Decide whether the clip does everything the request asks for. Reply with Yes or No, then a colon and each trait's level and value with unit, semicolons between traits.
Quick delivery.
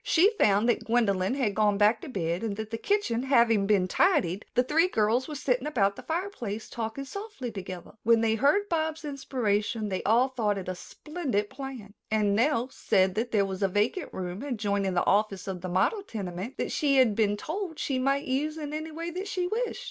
Yes: fast, 210 wpm